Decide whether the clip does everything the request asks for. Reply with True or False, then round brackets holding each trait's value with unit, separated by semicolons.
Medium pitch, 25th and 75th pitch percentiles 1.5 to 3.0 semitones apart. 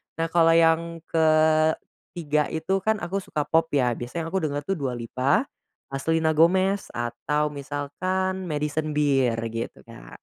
True (155 Hz; 2.7 semitones)